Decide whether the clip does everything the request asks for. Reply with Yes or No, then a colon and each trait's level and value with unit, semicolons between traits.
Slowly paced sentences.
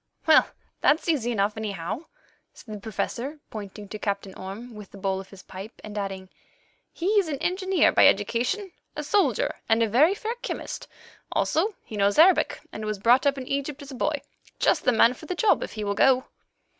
No: average, 195 wpm